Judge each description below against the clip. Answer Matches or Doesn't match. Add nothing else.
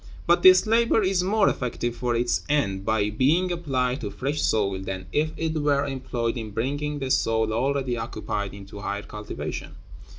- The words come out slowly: Doesn't match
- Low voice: Matches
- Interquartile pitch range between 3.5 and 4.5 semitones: Doesn't match